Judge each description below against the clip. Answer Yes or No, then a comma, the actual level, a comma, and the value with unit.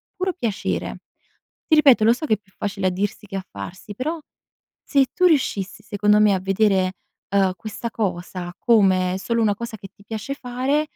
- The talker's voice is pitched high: Yes, high, 210 Hz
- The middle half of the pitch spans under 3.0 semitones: No, average, 4.2 semitones